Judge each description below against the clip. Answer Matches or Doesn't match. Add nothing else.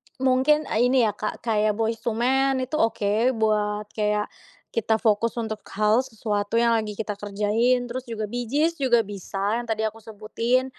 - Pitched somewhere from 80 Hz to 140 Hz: Doesn't match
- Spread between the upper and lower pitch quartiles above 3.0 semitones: Doesn't match